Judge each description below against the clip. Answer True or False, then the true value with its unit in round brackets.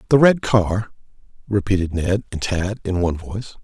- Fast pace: False (165 wpm)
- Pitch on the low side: True (100 Hz)